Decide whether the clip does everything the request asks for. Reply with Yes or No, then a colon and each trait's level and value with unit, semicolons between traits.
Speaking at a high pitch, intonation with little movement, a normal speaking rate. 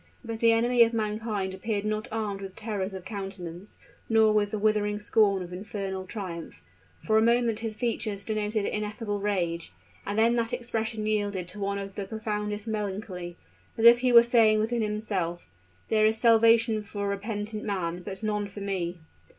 Yes: high, 210 Hz; narrow, 2.0 semitones; average, 175 wpm